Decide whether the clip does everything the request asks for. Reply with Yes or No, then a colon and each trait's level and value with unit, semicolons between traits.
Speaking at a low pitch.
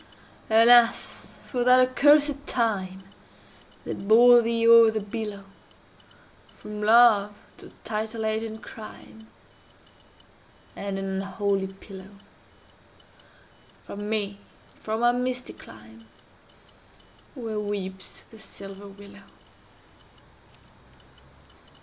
No: high, 215 Hz